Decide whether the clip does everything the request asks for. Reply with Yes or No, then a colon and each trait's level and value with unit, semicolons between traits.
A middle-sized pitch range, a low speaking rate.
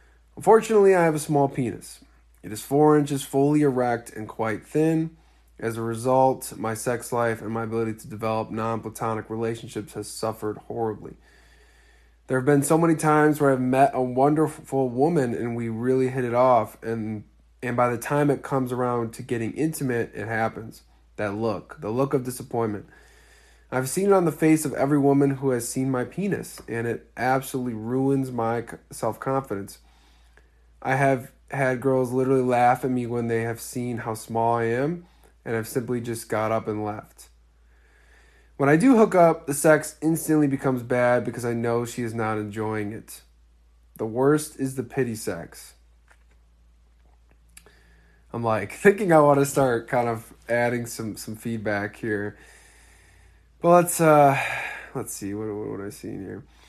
No: average, 4.2 semitones; average, 170 wpm